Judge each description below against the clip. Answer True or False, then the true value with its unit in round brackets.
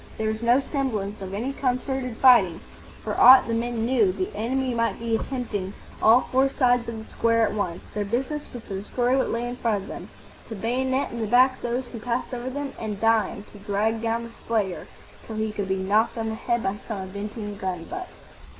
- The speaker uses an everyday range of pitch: True (3.2 semitones)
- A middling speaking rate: False (215 wpm)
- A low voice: False (230 Hz)